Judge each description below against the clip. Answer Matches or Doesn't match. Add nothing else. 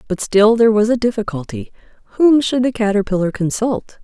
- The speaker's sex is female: Matches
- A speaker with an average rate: Matches